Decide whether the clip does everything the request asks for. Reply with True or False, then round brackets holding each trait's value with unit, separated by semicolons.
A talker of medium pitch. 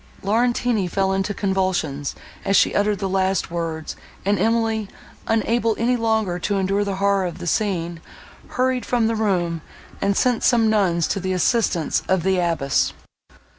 False (195 Hz)